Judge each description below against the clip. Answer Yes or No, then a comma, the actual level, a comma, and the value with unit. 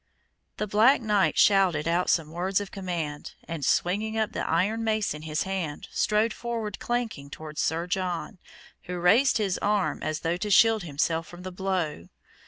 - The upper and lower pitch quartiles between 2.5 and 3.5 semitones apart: No, average, 4.3 semitones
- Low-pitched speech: No, medium, 185 Hz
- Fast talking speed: No, average, 175 wpm